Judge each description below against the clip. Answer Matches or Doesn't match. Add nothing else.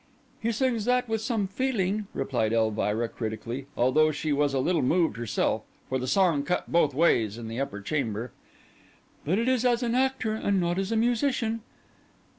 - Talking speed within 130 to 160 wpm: Doesn't match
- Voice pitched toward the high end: Doesn't match